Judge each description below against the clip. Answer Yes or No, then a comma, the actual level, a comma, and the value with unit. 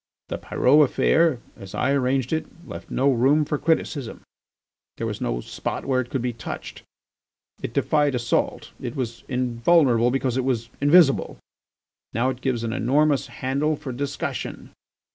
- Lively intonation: No, average, 3.1 semitones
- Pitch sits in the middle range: No, low, 130 Hz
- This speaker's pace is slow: No, average, 155 wpm